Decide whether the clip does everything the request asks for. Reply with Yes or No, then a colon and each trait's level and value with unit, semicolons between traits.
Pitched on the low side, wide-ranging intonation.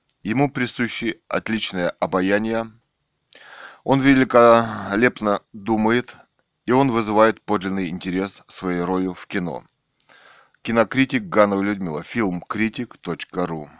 No: low, 110 Hz; average, 3.7 semitones